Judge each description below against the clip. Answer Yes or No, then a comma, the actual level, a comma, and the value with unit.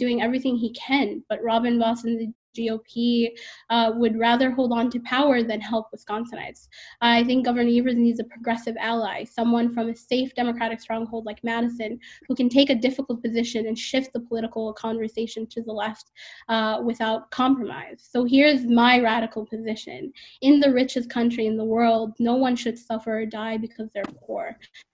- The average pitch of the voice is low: No, high, 230 Hz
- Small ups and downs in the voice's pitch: Yes, narrow, 1.7 semitones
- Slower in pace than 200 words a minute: Yes, average, 180 wpm